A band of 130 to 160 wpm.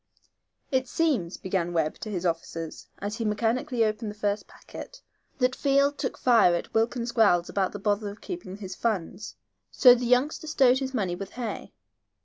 No: average, 175 wpm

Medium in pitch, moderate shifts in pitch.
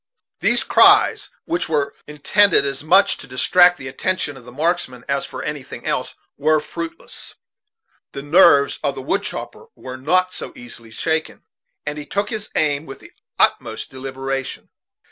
Yes: medium, 150 Hz; average, 4.9 semitones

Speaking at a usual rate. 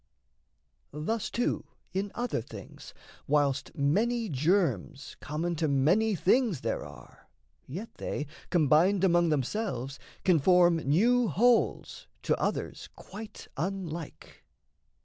No: slow, 110 wpm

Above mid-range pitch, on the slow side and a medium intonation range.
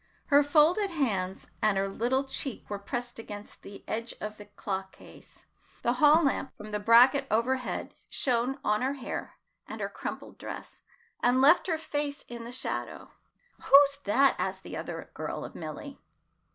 No: high, 245 Hz; average, 165 wpm; average, 4.8 semitones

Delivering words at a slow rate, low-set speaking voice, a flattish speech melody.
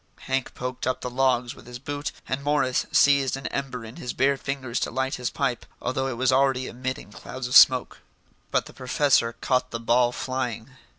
No: average, 195 wpm; low, 130 Hz; narrow, 1.4 semitones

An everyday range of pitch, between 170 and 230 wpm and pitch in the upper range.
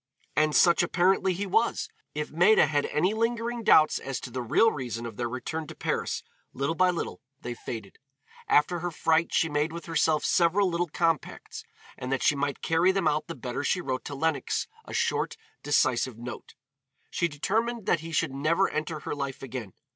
No: average, 4.5 semitones; average, 190 wpm; medium, 160 Hz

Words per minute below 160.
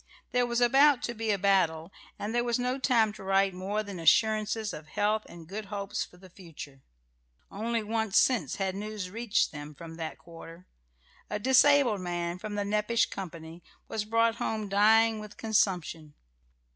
No: average, 170 wpm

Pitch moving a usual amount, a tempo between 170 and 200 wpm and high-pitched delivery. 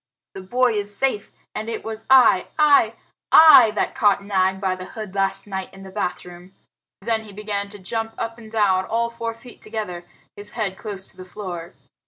Yes: average, 3.0 semitones; average, 195 wpm; high, 205 Hz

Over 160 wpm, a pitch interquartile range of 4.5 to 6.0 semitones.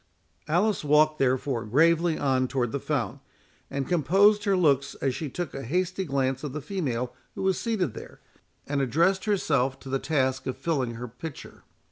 Yes: average, 175 wpm; average, 5.0 semitones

